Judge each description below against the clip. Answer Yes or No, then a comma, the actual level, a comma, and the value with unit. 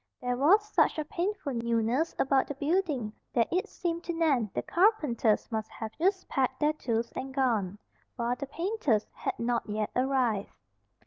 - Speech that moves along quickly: No, average, 170 wpm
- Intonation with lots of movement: Yes, wide, 6.2 semitones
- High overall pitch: Yes, very high, 265 Hz